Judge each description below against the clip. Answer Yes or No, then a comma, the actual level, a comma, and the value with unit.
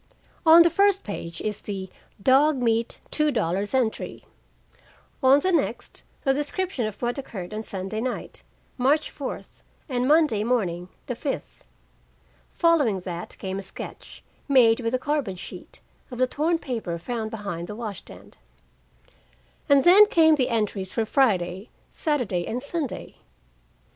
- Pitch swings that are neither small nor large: No, wide, 6.1 semitones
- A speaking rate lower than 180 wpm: Yes, average, 145 wpm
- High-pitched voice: Yes, high, 245 Hz